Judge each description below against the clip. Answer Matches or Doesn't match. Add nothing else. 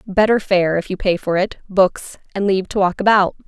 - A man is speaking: Doesn't match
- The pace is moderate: Doesn't match